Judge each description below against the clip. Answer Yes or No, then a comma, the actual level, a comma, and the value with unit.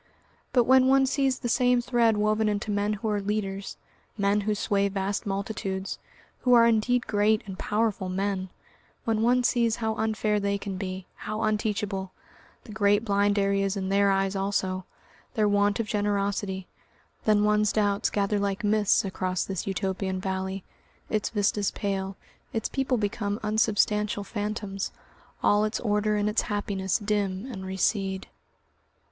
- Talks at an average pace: Yes, average, 150 wpm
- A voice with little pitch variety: Yes, narrow, 1.7 semitones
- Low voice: No, high, 205 Hz